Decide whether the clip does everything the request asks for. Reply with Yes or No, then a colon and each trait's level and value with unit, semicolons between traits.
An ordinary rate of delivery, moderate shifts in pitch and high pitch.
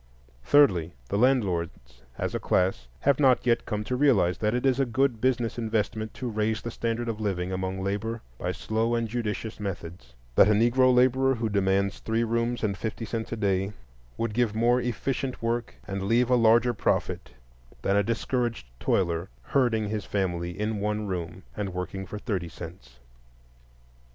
No: average, 175 wpm; average, 3.7 semitones; low, 110 Hz